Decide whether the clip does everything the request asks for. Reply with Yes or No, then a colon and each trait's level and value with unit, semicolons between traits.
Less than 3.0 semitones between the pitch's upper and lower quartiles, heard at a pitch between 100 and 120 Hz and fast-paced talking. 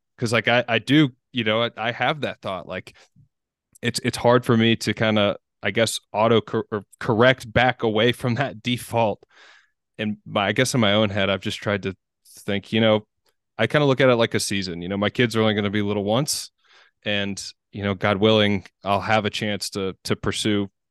Yes: narrow, 2.6 semitones; low, 110 Hz; fast, 225 wpm